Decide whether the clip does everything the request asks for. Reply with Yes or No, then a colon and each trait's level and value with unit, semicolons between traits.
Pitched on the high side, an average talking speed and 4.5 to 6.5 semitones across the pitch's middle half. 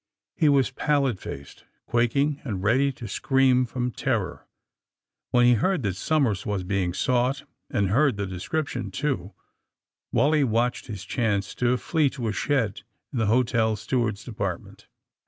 No: low, 120 Hz; average, 155 wpm; average, 4.9 semitones